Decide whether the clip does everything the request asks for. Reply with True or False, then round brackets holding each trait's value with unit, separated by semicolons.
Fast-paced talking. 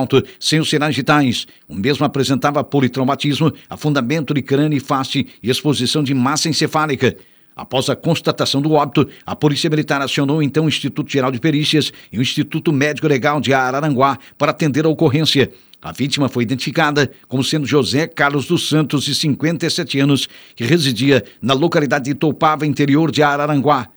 False (165 wpm)